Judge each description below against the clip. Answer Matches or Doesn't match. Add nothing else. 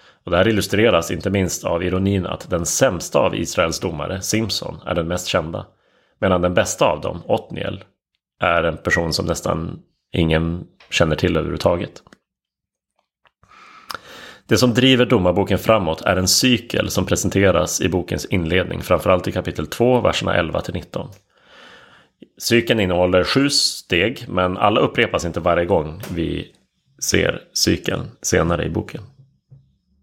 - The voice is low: Matches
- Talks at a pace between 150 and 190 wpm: Doesn't match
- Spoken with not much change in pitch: Doesn't match